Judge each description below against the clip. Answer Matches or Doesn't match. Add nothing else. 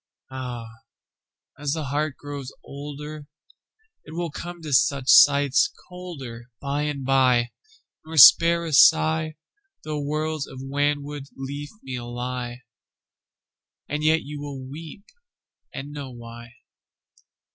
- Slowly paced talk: Matches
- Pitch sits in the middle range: Matches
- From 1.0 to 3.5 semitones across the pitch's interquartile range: Matches